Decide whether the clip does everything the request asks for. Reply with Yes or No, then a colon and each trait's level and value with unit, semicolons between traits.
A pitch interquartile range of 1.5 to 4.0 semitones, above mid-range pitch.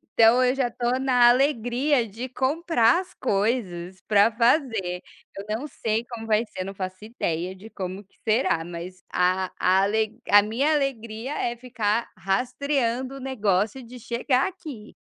No: average, 4.4 semitones; high, 230 Hz